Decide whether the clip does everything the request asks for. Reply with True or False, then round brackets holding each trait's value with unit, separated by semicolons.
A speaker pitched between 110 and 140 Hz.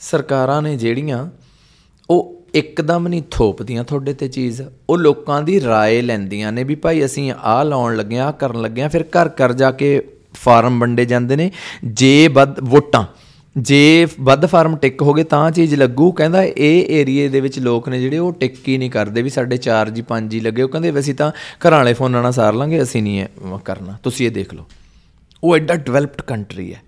True (135 Hz)